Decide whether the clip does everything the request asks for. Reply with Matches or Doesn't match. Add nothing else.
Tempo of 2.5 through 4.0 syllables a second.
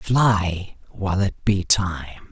Matches